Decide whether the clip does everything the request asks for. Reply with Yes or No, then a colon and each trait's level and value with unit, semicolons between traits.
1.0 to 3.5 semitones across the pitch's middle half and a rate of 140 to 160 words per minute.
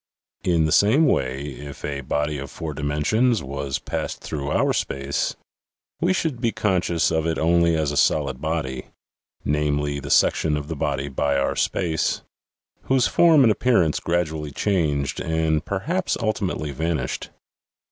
No: average, 4.0 semitones; average, 155 wpm